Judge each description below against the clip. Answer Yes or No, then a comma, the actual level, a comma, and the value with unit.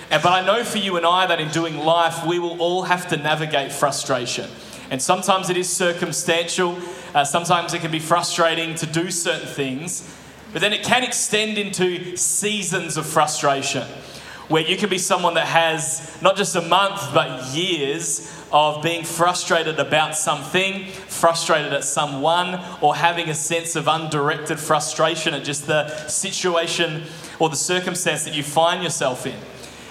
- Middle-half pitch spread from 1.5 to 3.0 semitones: Yes, narrow, 2.5 semitones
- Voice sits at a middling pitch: Yes, medium, 165 Hz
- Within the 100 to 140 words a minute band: No, average, 165 wpm